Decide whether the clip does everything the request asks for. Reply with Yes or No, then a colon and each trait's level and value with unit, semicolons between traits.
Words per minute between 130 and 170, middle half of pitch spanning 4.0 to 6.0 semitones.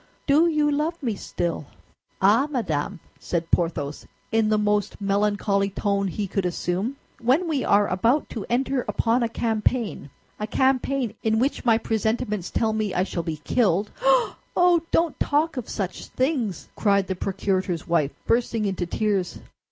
Yes: average, 150 wpm; average, 4.9 semitones